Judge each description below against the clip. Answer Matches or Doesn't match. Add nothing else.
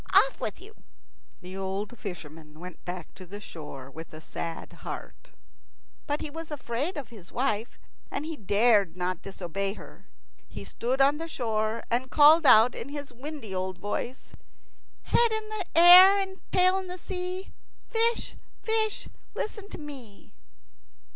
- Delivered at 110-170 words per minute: Matches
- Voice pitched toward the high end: Matches